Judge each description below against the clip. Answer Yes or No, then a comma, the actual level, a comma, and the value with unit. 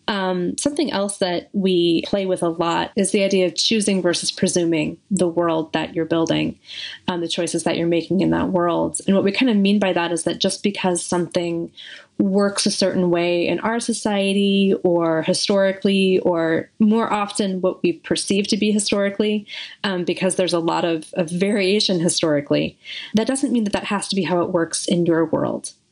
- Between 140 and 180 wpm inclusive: No, average, 195 wpm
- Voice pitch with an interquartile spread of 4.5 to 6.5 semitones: No, average, 2.8 semitones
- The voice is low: No, medium, 185 Hz